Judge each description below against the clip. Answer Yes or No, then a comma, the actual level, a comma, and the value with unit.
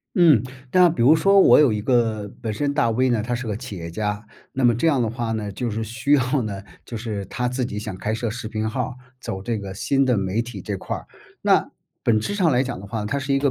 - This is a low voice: Yes, low, 115 Hz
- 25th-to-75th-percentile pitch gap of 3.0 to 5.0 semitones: Yes, average, 3.6 semitones